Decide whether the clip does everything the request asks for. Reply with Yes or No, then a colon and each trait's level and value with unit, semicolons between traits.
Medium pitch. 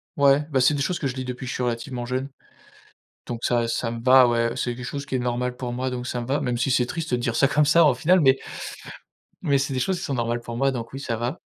No: low, 125 Hz